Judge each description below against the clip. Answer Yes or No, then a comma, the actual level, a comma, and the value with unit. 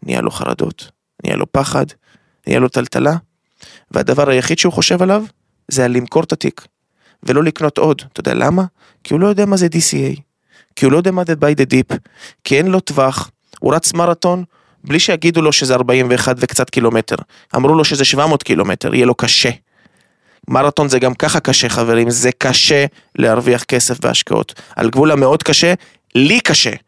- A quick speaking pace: Yes, fast, 180 wpm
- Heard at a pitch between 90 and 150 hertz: Yes, medium, 140 Hz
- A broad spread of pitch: No, average, 4.6 semitones